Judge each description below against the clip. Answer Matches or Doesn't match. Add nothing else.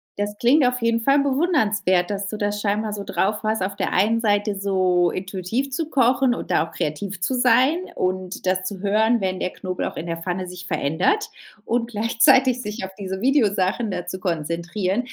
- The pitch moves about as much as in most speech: Matches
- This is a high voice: Matches